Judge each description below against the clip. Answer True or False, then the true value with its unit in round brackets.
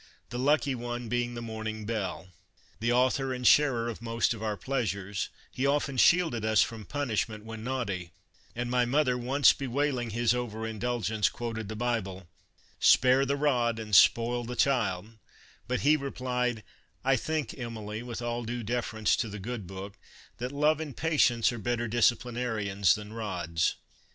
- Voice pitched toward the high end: False (120 Hz)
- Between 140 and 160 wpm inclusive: False (170 wpm)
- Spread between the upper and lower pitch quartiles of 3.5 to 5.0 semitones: False (2.5 semitones)